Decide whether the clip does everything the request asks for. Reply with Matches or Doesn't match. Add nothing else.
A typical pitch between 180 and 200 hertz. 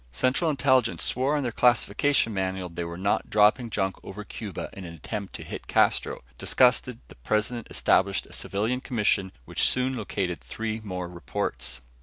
Doesn't match